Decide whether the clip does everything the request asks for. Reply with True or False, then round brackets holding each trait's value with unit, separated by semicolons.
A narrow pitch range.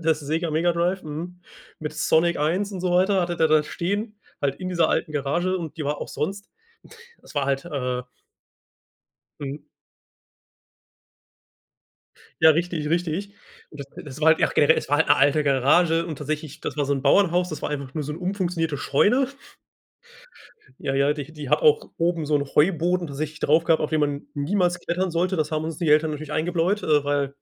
False (3.0 semitones)